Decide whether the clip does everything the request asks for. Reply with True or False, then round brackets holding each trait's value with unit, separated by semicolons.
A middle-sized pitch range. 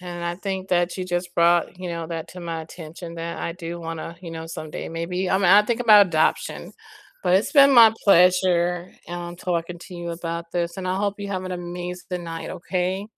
False (1.7 semitones)